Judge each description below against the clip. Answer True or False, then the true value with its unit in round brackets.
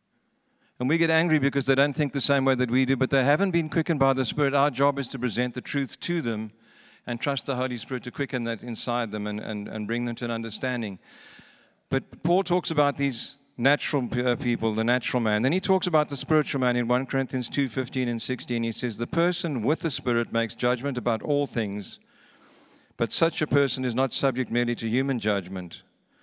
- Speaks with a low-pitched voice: True (130 Hz)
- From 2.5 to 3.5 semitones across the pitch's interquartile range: True (3.1 semitones)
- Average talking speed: False (215 wpm)